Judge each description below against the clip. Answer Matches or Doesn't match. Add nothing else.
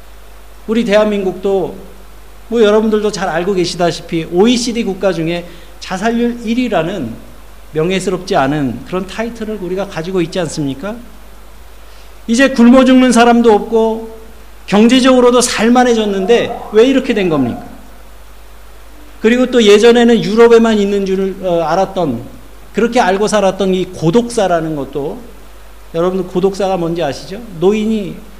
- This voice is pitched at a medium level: Doesn't match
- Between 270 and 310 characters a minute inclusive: Matches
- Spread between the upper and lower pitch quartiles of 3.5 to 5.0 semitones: Matches